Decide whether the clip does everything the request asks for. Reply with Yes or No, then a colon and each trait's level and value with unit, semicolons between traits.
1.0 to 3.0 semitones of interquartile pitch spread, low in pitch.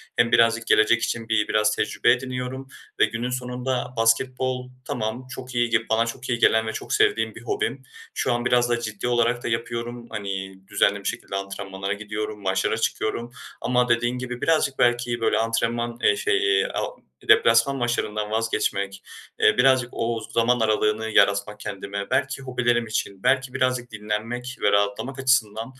Yes: average, 2.7 semitones; low, 120 Hz